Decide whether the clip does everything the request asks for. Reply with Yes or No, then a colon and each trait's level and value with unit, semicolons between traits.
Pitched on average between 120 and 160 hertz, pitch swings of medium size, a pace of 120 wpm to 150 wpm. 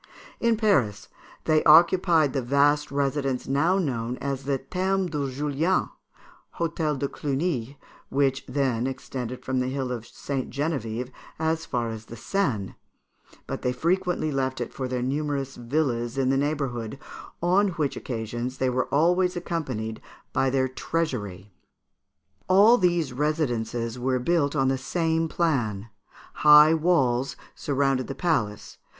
Yes: low, 135 Hz; average, 4.2 semitones; average, 140 wpm